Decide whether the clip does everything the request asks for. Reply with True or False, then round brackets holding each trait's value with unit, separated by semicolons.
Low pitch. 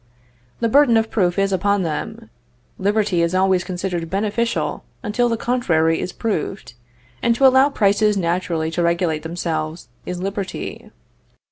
False (190 Hz)